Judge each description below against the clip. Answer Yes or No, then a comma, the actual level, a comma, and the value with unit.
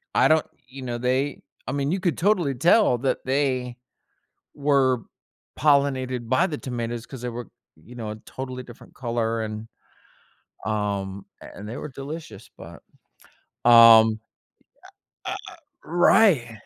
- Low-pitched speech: Yes, low, 125 Hz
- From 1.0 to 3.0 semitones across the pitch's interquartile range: No, average, 3.5 semitones